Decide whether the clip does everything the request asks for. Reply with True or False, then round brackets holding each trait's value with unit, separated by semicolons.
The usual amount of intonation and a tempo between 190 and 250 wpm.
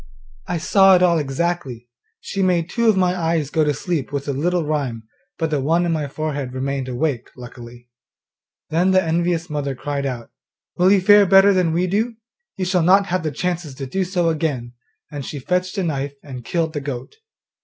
True (4.6 semitones; 200 wpm)